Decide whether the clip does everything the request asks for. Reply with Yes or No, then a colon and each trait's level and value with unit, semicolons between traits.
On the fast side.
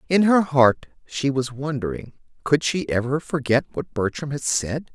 No: average, 170 wpm